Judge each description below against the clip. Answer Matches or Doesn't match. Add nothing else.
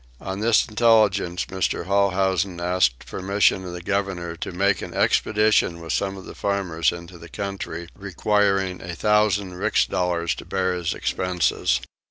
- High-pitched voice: Doesn't match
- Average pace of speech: Matches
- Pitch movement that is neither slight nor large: Doesn't match